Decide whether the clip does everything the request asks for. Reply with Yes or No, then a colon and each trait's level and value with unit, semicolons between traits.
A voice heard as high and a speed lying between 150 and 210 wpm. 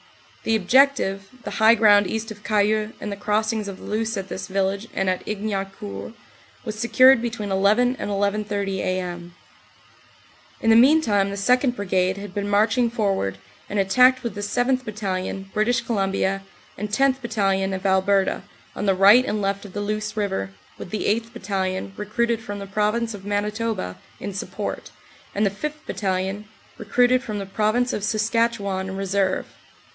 Yes: high, 205 Hz; average, 170 wpm